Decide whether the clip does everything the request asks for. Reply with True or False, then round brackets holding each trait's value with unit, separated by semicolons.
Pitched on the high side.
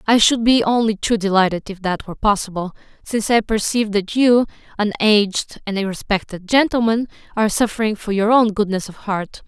True (210 Hz)